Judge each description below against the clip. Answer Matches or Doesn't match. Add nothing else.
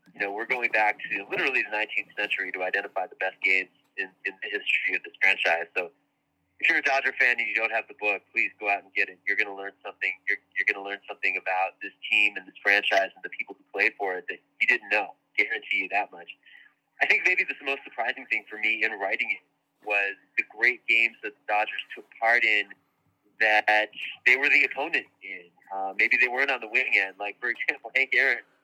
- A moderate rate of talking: Doesn't match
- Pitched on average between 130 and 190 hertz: Doesn't match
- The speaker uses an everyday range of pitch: Doesn't match